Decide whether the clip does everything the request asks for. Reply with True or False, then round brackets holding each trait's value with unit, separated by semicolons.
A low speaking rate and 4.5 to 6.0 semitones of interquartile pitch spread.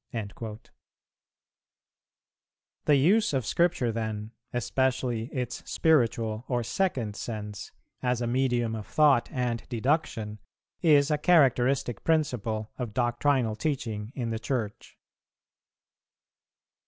False (105 wpm; 3.8 semitones)